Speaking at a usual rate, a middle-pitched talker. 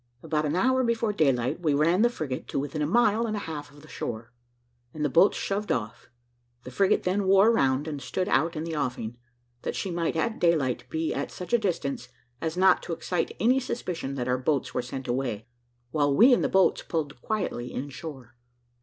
No: fast, 210 wpm; medium, 160 Hz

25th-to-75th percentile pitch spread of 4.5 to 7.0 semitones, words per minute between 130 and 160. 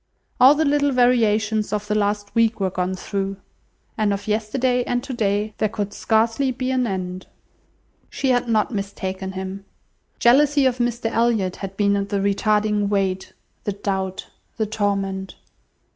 No: average, 3.3 semitones; average, 150 wpm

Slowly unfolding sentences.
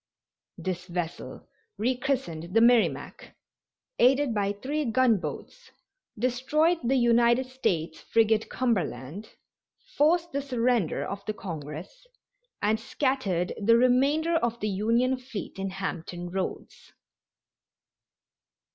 Yes: slow, 105 wpm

